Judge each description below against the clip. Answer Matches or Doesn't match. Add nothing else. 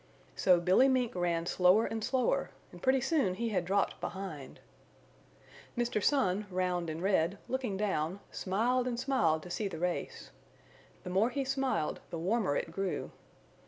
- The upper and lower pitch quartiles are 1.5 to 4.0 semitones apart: Doesn't match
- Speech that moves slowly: Doesn't match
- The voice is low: Doesn't match